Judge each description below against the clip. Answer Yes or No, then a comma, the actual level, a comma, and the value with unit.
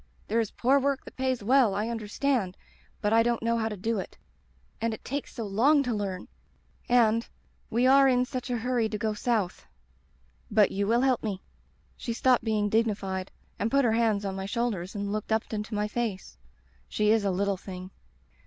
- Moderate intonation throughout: Yes, average, 3.1 semitones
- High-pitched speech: Yes, high, 220 Hz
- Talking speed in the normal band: No, fast, 210 wpm